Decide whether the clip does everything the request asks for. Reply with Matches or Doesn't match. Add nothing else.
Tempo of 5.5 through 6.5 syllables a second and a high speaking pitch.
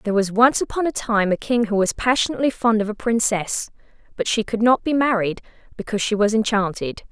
Matches